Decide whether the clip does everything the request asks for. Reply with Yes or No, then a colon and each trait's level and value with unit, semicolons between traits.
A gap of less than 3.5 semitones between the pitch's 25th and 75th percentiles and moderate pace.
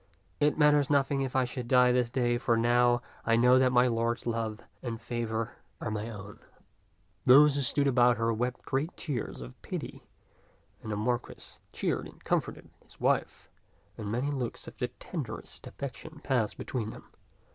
Yes: narrow, 2.5 semitones; average, 170 wpm